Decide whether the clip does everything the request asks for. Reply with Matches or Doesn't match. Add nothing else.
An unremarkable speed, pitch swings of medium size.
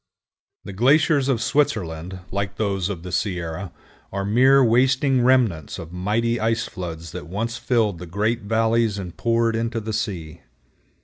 Matches